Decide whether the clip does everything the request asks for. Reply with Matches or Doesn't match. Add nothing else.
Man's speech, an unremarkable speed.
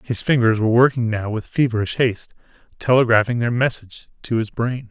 Matches